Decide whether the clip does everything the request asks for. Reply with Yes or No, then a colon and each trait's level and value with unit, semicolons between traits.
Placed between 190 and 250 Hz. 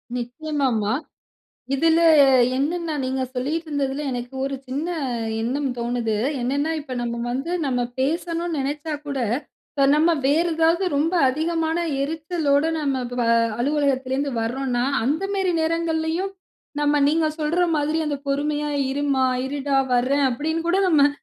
No: very high, 290 Hz